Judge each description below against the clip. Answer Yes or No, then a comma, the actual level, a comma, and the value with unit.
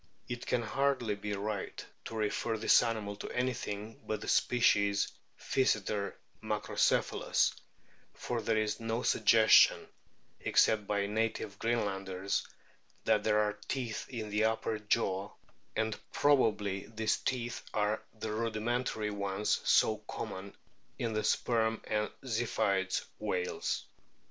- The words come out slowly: Yes, slow, 120 wpm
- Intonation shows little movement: Yes, narrow, 1.9 semitones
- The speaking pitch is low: Yes, low, 110 Hz